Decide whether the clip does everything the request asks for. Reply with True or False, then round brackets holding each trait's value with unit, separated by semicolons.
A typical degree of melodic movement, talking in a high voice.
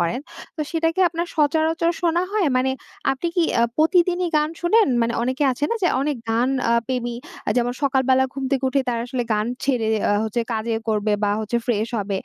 False (5.7 semitones; 265 Hz)